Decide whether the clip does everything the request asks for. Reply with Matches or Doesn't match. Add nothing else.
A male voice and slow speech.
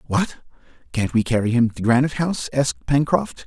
Doesn't match